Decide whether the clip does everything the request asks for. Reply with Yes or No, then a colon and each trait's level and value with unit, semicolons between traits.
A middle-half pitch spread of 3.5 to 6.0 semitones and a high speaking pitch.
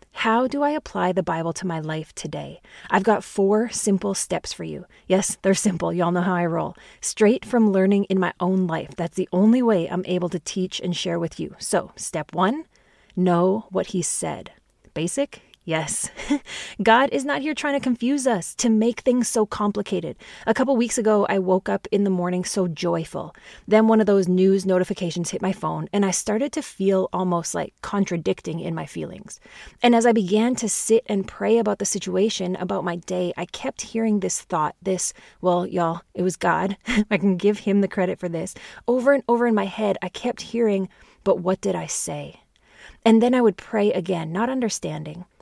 Yes: average, 3.8 semitones; high, 195 Hz